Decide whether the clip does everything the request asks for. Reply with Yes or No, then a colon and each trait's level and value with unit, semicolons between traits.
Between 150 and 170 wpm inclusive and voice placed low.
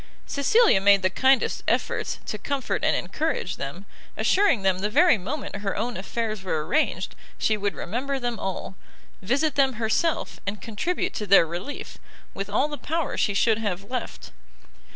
No: average, 165 wpm; high, 225 Hz